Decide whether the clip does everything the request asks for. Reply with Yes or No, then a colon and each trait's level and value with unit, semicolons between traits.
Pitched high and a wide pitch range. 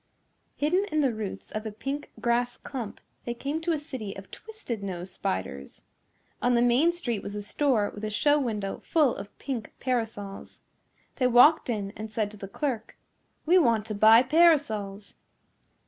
Yes: high, 235 Hz; wide, 5.7 semitones